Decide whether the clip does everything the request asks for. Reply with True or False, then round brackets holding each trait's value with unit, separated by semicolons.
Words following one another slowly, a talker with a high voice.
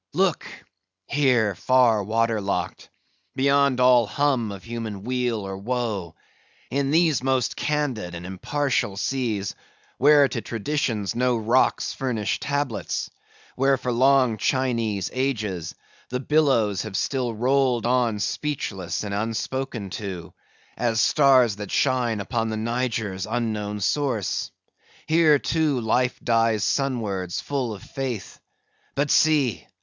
False (125 wpm; 120 Hz)